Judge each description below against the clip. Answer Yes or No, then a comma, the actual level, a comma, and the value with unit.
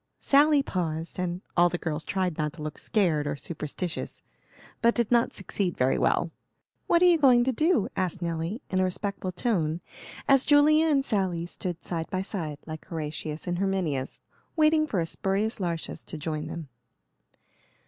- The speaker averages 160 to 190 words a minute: Yes, average, 170 wpm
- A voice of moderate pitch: Yes, medium, 180 Hz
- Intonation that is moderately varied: No, wide, 6.4 semitones